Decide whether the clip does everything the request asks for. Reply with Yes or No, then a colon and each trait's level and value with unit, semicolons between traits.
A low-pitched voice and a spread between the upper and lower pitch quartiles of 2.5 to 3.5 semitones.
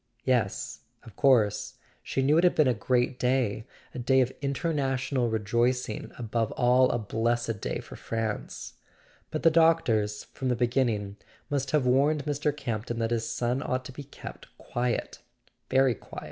Yes: low, 125 Hz; average, 2.9 semitones